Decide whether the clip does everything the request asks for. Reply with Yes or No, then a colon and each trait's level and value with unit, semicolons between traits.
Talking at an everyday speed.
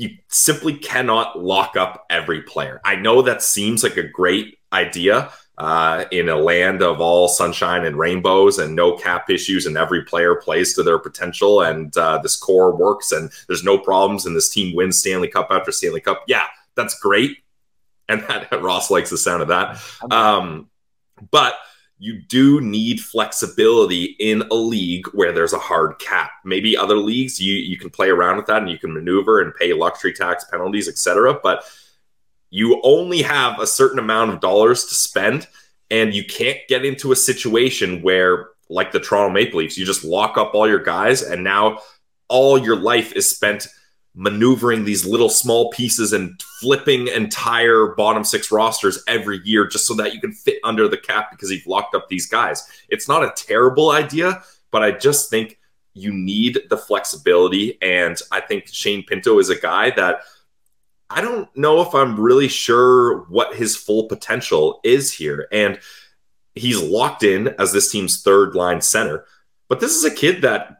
Yes: average, 185 wpm